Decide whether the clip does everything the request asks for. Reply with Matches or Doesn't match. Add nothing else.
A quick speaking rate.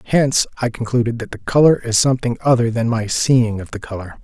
Matches